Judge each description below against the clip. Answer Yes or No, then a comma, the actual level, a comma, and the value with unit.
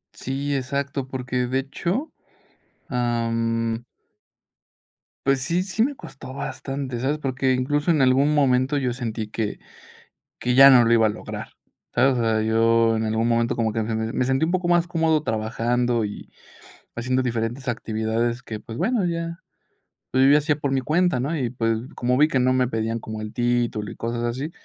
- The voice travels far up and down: No, average, 3.3 semitones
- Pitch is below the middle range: Yes, low, 125 Hz